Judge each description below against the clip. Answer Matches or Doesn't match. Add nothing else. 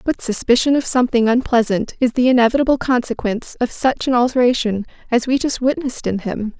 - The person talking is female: Matches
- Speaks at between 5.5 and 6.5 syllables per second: Matches